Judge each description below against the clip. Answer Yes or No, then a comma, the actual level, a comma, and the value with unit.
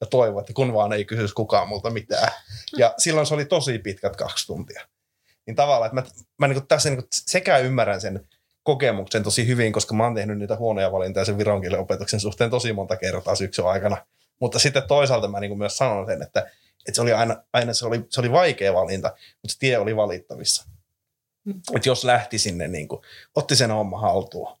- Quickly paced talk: Yes, fast, 200 wpm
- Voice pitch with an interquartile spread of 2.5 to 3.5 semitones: No, average, 4.0 semitones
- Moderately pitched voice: No, low, 115 Hz